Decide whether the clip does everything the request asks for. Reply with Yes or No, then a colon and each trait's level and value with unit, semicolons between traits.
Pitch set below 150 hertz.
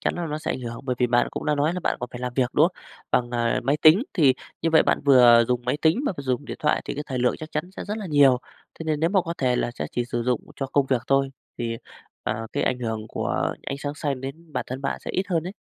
Yes: low, 135 Hz